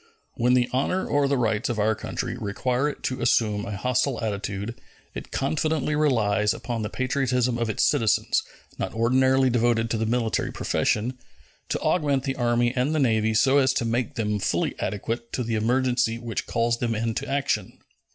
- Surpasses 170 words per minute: Yes, average, 180 wpm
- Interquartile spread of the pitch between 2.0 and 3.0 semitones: Yes, average, 2.7 semitones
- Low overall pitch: Yes, low, 120 Hz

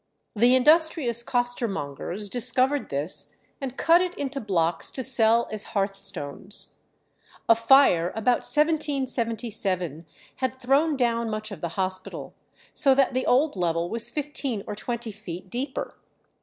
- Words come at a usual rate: No, slow, 130 wpm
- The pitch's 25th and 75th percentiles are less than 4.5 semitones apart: No, average, 5.1 semitones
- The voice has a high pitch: Yes, high, 235 Hz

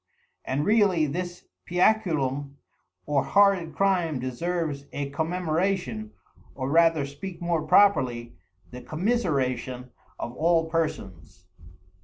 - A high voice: No, medium, 160 Hz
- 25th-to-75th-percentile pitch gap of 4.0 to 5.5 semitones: Yes, average, 5.1 semitones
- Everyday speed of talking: No, slow, 100 wpm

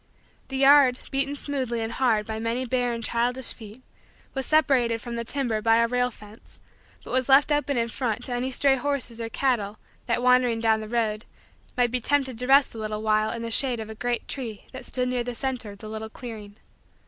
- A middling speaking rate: No, fast, 215 wpm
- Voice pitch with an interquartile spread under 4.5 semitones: Yes, narrow, 2.6 semitones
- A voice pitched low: No, high, 240 Hz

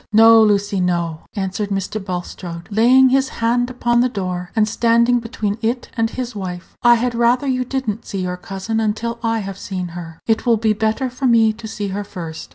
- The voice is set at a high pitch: Yes, high, 220 Hz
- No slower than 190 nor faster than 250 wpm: Yes, fast, 205 wpm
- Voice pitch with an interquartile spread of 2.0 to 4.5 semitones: Yes, average, 3.6 semitones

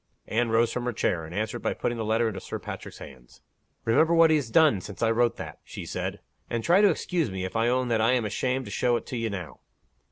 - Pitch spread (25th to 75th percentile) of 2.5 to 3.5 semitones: Yes, average, 2.8 semitones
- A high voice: No, low, 115 Hz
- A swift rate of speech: Yes, fast, 260 wpm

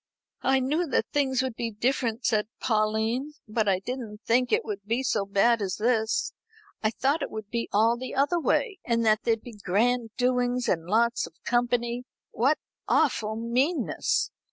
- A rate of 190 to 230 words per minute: No, average, 175 wpm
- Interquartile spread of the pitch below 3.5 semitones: Yes, average, 2.8 semitones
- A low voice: No, high, 235 Hz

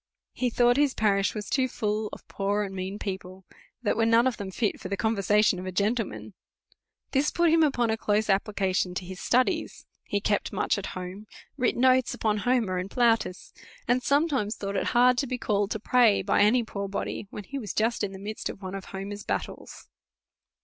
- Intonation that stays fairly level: No, average, 3.6 semitones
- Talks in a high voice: Yes, high, 210 Hz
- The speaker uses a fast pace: Yes, fast, 215 wpm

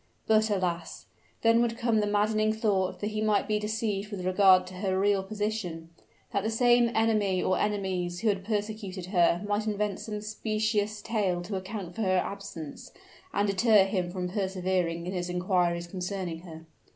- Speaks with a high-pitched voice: Yes, high, 200 Hz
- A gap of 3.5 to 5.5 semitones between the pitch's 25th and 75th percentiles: No, average, 2.7 semitones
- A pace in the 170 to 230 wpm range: Yes, average, 175 wpm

